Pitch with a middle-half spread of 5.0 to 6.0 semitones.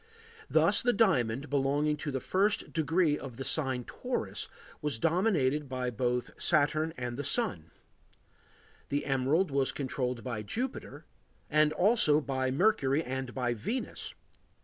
No: average, 3.8 semitones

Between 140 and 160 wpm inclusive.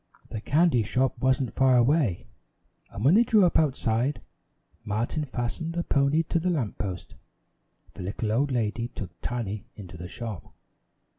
Yes: average, 155 wpm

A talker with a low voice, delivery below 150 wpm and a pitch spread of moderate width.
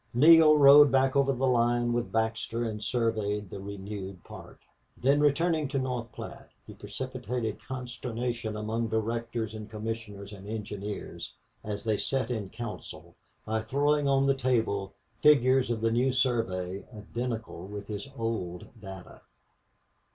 Yes: low, 115 Hz; average, 140 wpm; average, 3.5 semitones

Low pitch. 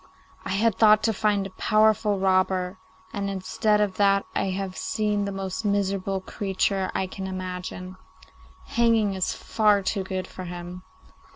No: high, 195 Hz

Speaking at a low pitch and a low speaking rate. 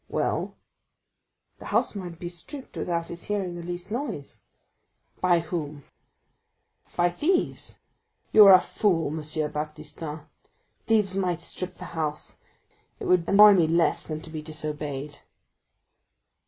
No: medium, 170 Hz; slow, 125 wpm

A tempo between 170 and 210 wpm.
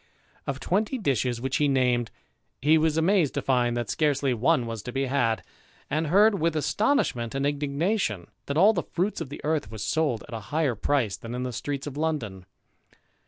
Yes: average, 195 wpm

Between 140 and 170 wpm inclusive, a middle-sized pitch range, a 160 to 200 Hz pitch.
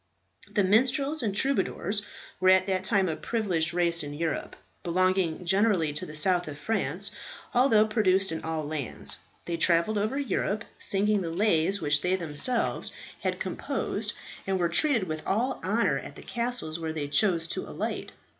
Yes: average, 165 wpm; average, 4.6 semitones; medium, 185 Hz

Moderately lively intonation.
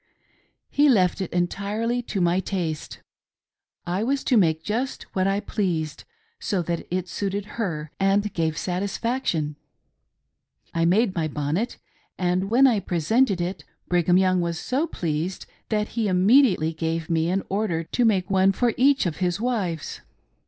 Yes: average, 4.1 semitones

